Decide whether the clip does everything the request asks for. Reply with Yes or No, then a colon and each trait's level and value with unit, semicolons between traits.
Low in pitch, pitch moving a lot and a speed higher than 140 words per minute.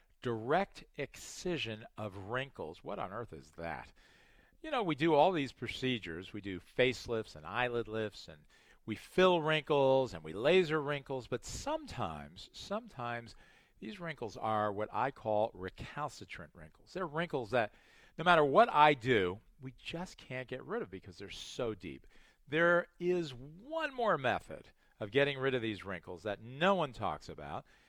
Yes: low, 125 Hz; wide, 6.4 semitones; average, 160 wpm